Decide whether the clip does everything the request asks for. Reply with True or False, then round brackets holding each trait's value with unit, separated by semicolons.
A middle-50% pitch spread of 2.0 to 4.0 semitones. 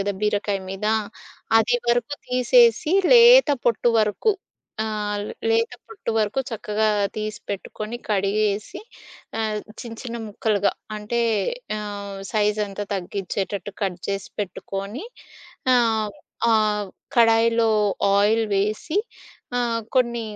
True (2.6 semitones)